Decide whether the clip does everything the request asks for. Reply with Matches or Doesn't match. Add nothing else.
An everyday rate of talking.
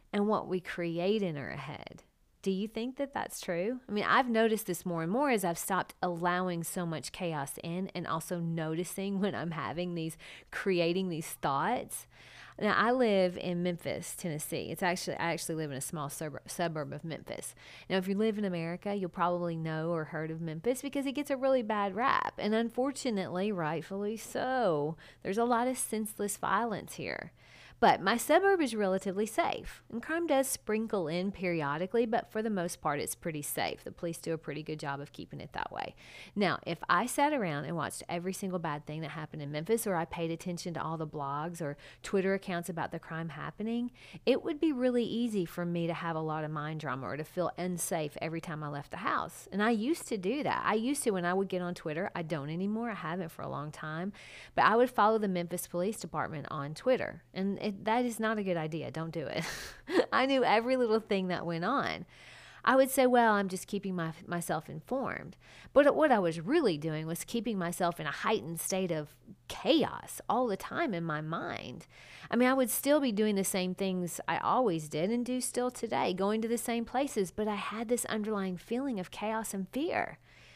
Doesn't match